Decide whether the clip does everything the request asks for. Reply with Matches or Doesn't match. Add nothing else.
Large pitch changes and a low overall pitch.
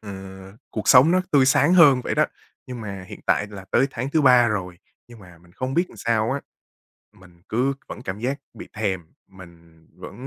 Matches